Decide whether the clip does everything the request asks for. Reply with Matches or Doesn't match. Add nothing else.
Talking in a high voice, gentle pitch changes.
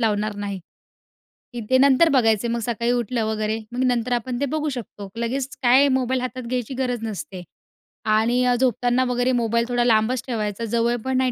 Matches